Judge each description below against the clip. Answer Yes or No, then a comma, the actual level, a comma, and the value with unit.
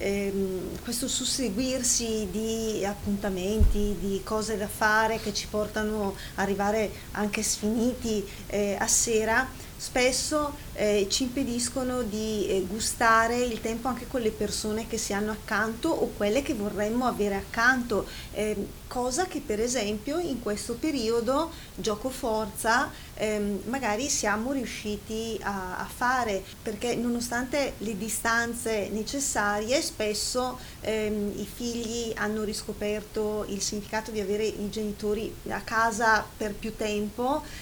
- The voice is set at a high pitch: Yes, high, 220 Hz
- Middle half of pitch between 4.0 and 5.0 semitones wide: No, narrow, 2.5 semitones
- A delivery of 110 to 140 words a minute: Yes, average, 130 wpm